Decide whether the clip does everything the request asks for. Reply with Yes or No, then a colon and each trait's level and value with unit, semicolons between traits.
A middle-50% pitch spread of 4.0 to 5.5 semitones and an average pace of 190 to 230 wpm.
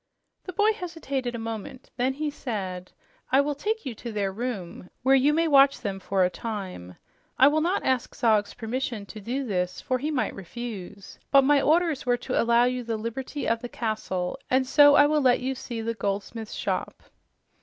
Yes: average, 4.5 semitones; average, 195 wpm